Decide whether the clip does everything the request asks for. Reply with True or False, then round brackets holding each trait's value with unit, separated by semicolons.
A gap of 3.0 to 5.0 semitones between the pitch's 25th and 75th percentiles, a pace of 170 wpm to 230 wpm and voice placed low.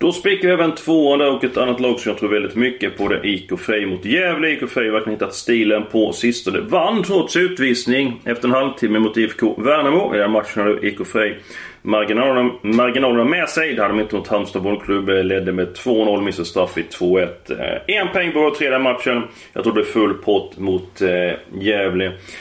True (4.1 semitones; 195 wpm; 115 Hz)